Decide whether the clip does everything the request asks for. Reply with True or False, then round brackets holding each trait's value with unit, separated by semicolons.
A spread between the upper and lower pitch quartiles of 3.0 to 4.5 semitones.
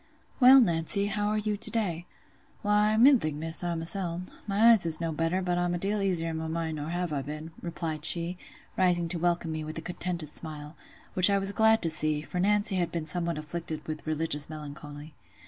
True (3.7 semitones)